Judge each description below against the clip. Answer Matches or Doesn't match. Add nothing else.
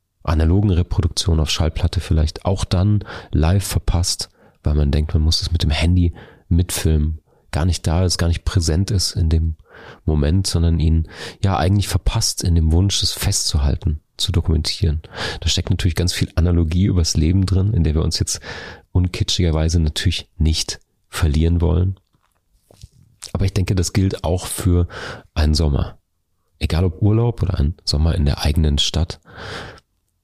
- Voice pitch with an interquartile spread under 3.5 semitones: Matches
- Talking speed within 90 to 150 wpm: Doesn't match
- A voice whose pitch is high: Doesn't match